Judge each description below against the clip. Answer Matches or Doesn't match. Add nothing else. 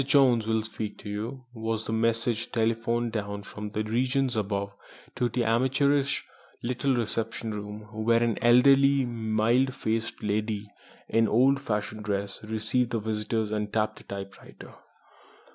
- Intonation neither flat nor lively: Doesn't match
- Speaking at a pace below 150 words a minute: Matches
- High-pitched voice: Doesn't match